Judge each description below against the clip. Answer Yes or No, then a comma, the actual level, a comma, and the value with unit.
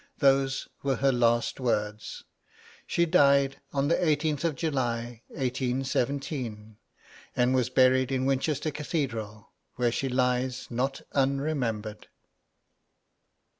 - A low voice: Yes, low, 130 Hz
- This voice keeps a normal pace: No, slow, 105 wpm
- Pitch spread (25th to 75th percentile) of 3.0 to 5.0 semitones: No, narrow, 2.5 semitones